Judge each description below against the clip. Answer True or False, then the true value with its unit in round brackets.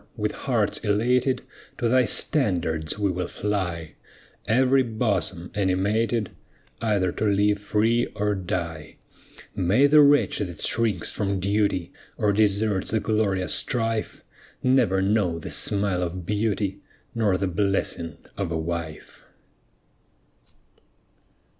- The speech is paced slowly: True (115 wpm)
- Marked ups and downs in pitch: False (3.3 semitones)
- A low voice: True (100 Hz)